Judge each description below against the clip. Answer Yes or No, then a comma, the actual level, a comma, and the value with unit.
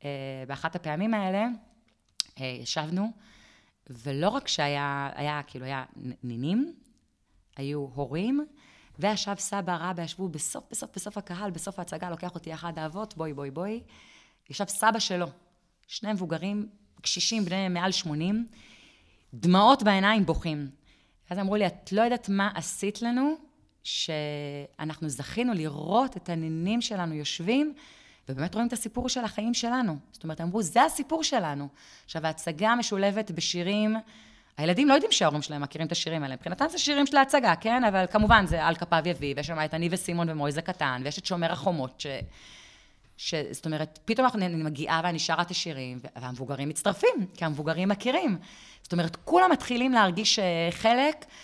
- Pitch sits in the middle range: Yes, medium, 180 Hz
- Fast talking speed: Yes, fast, 155 wpm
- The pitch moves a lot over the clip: Yes, wide, 6.0 semitones